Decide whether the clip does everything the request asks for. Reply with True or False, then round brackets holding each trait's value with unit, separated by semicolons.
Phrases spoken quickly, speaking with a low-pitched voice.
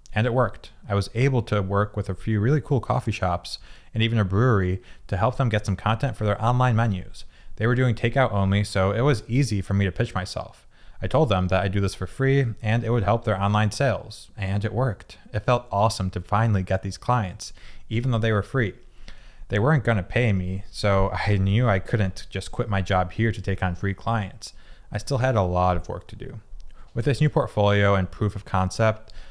True (230 wpm; 105 Hz)